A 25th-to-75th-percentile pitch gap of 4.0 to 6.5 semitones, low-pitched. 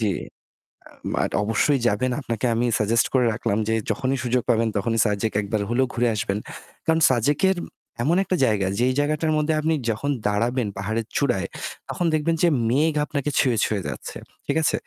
Yes: average, 5.0 semitones; low, 120 Hz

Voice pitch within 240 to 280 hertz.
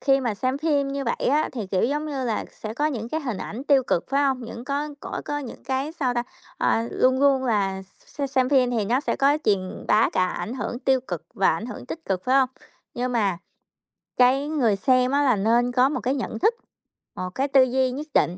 Yes: very high, 255 Hz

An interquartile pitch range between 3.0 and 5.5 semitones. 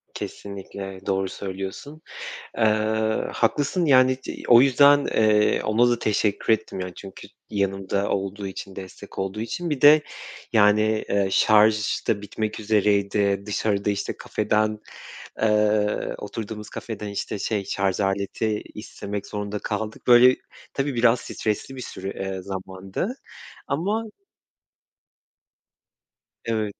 No: narrow, 2.4 semitones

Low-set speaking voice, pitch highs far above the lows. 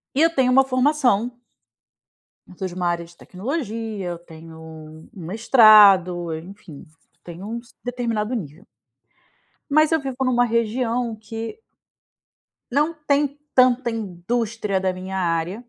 No: high, 220 Hz; wide, 5.9 semitones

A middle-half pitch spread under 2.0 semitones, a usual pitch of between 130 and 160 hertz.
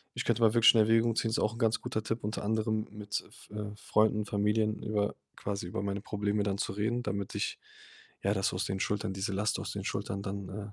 No: narrow, 1.5 semitones; low, 105 Hz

